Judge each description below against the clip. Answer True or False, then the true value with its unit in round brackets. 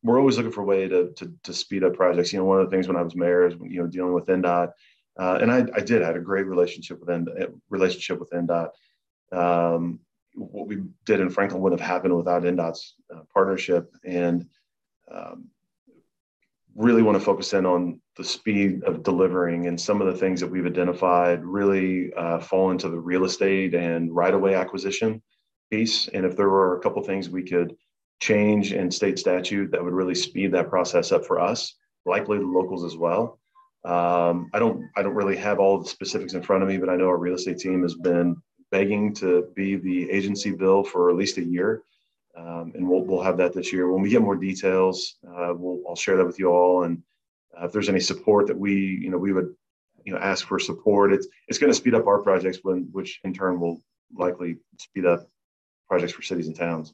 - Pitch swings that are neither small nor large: False (1.8 semitones)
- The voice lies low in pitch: True (90 Hz)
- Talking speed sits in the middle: False (220 wpm)